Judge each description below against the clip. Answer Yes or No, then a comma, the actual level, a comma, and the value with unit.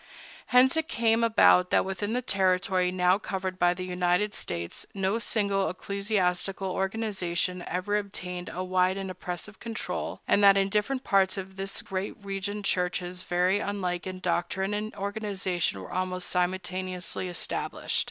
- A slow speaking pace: No, average, 150 wpm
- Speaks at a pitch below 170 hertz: No, high, 190 Hz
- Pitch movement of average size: No, narrow, 2.0 semitones